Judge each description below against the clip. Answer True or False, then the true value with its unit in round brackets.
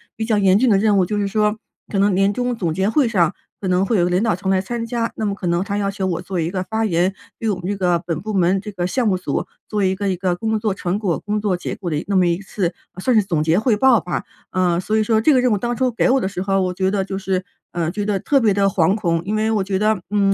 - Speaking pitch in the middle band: False (195 Hz)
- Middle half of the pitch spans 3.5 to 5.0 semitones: False (2.9 semitones)